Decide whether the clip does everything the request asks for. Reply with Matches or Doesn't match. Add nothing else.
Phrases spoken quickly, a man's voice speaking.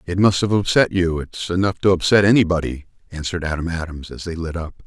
Doesn't match